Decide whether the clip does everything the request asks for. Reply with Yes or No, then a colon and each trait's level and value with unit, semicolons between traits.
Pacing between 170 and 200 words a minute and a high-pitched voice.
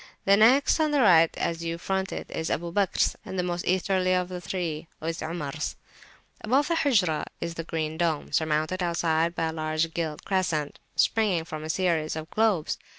No: average, 190 wpm; medium, 170 Hz